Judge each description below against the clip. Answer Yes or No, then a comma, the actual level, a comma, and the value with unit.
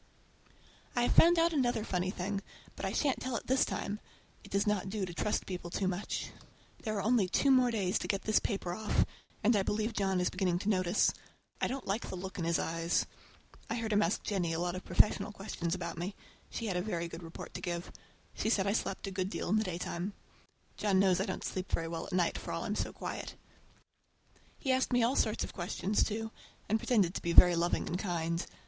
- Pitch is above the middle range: Yes, high, 195 Hz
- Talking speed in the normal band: No, fast, 230 wpm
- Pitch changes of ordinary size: Yes, average, 3.6 semitones